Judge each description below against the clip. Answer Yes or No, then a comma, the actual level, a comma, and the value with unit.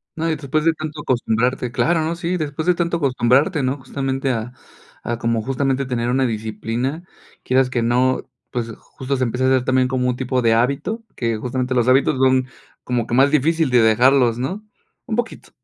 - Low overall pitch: Yes, low, 130 Hz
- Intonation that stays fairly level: No, average, 3.0 semitones